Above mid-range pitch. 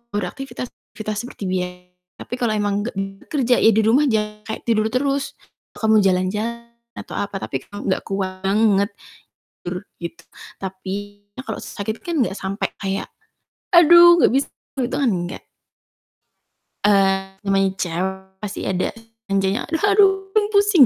Yes: high, 210 Hz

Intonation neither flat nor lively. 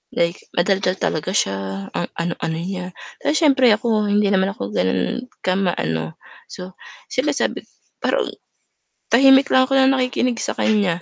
No: wide, 6.9 semitones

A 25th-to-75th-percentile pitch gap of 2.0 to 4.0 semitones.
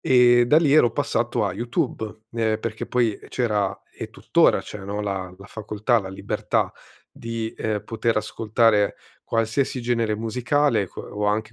Yes: narrow, 2.4 semitones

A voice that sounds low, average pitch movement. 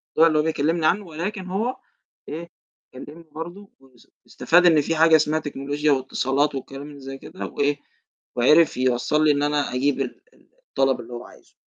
No: medium, 150 Hz; average, 3.3 semitones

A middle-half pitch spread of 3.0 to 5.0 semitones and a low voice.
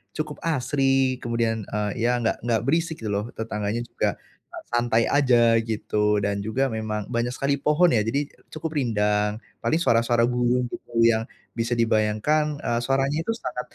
Yes: average, 3.7 semitones; low, 120 Hz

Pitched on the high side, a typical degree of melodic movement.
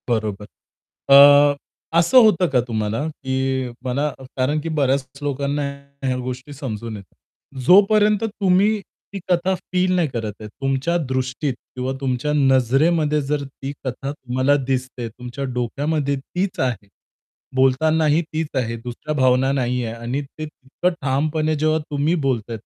No: low, 135 Hz; average, 3.4 semitones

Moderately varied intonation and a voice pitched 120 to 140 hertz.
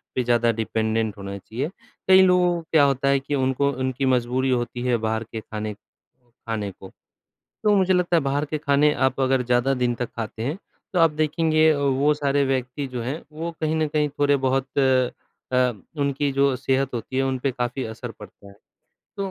Yes: average, 3.3 semitones; low, 135 Hz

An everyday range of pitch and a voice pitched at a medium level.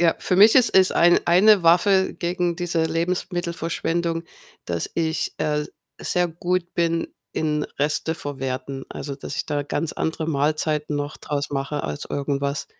Yes: average, 3.2 semitones; medium, 165 Hz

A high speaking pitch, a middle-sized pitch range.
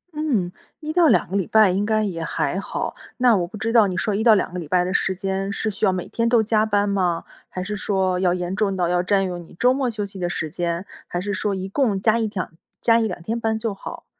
Yes: high, 200 Hz; average, 3.3 semitones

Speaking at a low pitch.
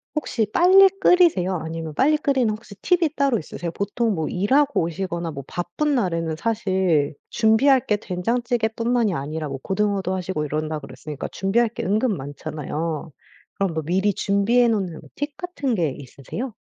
No: high, 195 Hz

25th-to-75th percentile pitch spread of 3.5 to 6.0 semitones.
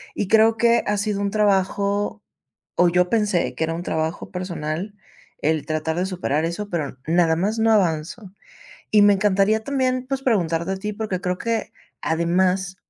Yes: average, 3.8 semitones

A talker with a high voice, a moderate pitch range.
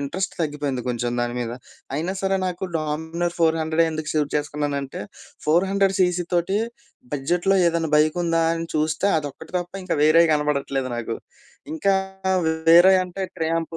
No: medium, 160 Hz; average, 3.0 semitones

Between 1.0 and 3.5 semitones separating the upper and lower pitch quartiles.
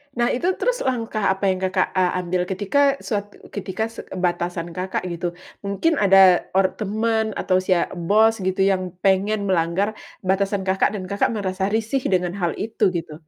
Yes: average, 2.8 semitones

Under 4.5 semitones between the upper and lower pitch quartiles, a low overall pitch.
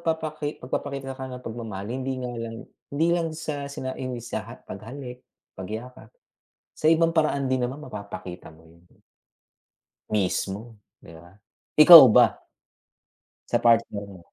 No: average, 5.1 semitones; low, 125 Hz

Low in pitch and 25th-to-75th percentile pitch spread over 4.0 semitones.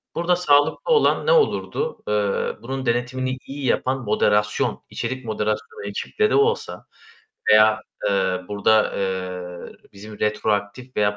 Yes: low, 110 Hz; average, 4.6 semitones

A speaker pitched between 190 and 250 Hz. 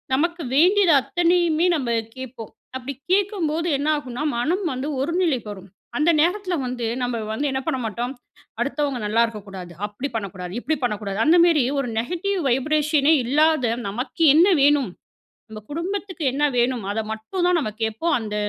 No: very high, 275 Hz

